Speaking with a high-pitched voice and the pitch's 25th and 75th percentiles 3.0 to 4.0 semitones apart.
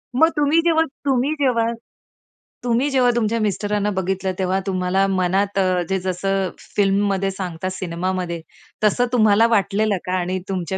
Yes: high, 195 Hz; average, 3.6 semitones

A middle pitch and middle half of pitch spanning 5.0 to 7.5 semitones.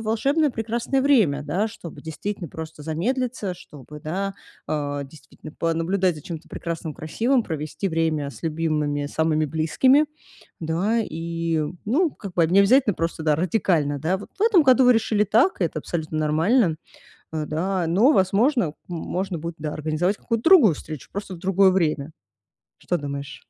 Yes: medium, 170 Hz; wide, 5.5 semitones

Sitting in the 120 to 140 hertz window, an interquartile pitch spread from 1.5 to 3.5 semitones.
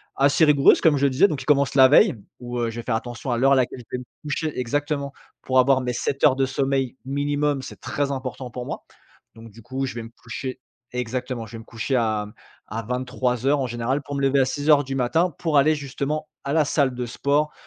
Yes: low, 135 Hz; narrow, 2.5 semitones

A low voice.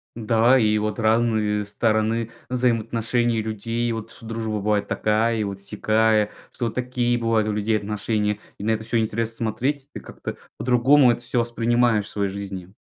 Yes: low, 110 Hz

